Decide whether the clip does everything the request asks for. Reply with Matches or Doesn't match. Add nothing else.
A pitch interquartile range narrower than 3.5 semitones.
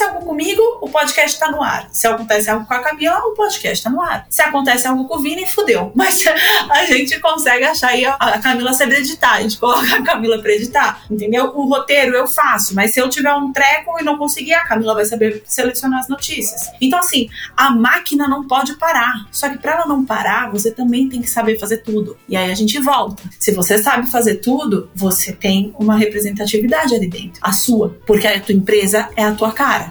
Doesn't match